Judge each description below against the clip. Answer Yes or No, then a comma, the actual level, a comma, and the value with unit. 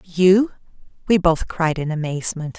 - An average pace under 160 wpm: Yes, average, 140 wpm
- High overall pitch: No, medium, 175 Hz